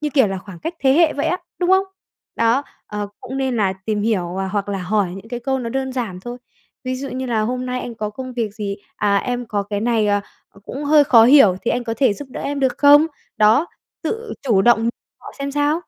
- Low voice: No, high, 240 Hz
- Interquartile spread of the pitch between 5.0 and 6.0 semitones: No, average, 4.5 semitones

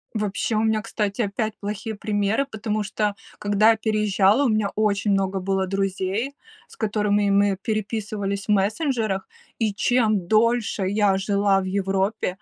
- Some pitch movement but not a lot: No, narrow, 1.7 semitones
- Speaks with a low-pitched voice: No, high, 205 Hz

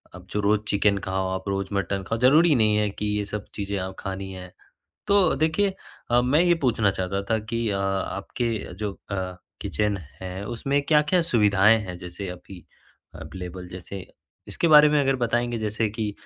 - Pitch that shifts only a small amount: No, average, 3.8 semitones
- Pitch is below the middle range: Yes, low, 105 Hz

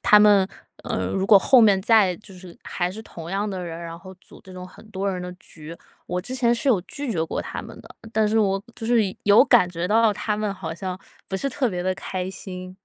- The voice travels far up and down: No, average, 3.0 semitones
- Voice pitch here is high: Yes, high, 195 Hz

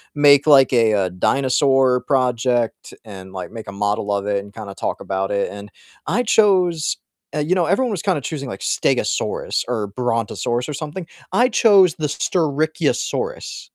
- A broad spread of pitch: Yes, wide, 7.3 semitones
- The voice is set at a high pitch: No, low, 130 Hz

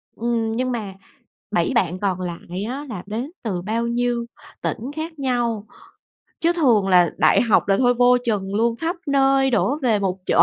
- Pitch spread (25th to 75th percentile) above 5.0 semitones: No, average, 4.3 semitones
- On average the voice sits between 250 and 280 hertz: No, high, 235 Hz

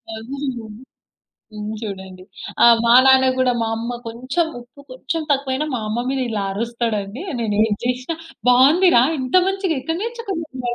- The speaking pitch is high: Yes, very high, 250 Hz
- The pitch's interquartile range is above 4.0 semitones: Yes, average, 4.5 semitones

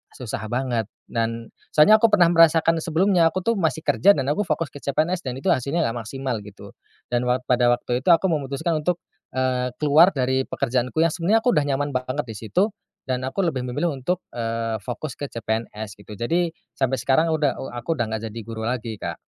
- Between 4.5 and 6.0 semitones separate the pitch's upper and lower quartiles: Yes, wide, 5.4 semitones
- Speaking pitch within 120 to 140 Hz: Yes, low, 135 Hz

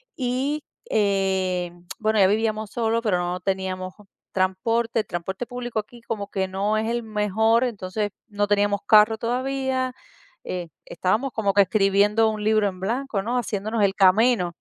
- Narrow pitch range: No, average, 3.2 semitones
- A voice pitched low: No, high, 210 Hz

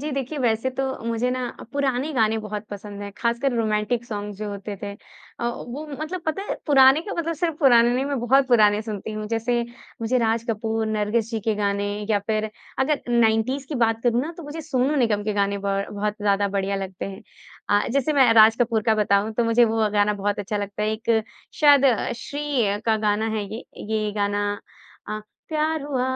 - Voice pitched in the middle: No, high, 225 Hz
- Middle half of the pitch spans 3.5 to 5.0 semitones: Yes, average, 4.0 semitones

